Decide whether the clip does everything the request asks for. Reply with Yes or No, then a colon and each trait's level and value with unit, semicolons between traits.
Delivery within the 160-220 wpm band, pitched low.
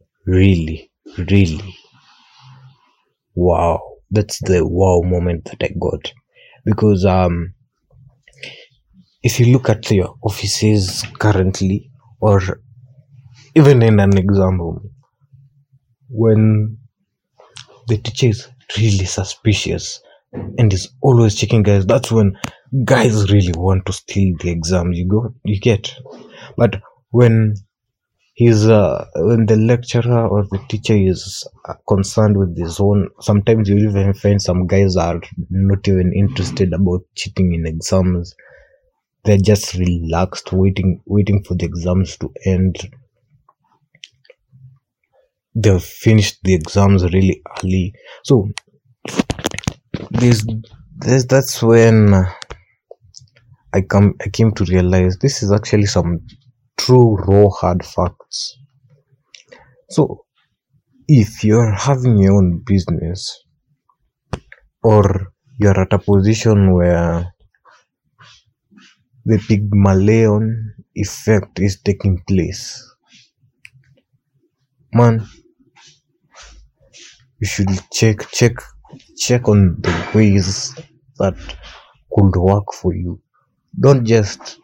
No: average, 105 wpm; low, 105 Hz